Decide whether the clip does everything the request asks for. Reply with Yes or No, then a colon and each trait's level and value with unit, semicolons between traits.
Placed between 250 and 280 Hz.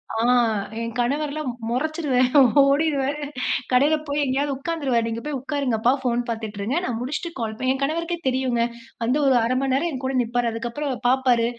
Yes: very high, 260 Hz